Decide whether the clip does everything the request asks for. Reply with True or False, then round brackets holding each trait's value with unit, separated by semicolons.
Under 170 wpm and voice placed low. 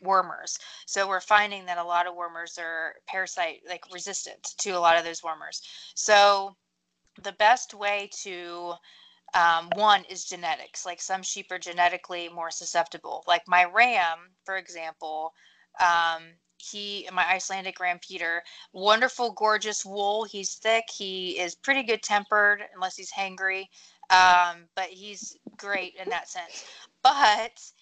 False (145 wpm; 185 Hz)